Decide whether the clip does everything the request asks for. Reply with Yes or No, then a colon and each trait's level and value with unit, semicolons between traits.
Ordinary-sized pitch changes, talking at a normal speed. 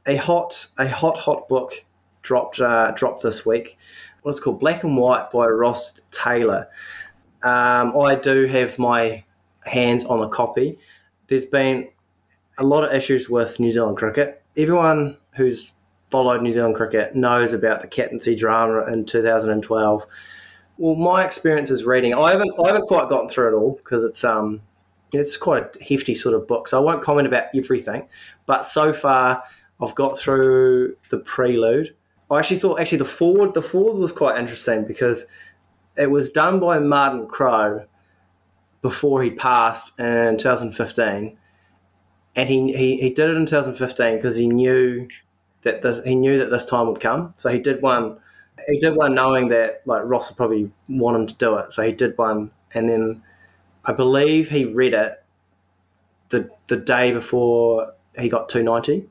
Yes: average, 3.6 semitones; average, 170 wpm